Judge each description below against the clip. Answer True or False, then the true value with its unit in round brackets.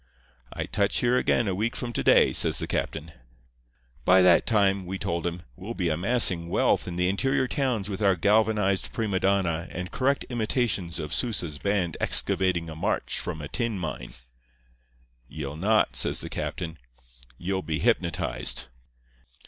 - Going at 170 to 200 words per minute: False (160 wpm)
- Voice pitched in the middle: False (95 Hz)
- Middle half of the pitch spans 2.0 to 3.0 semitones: False (4.4 semitones)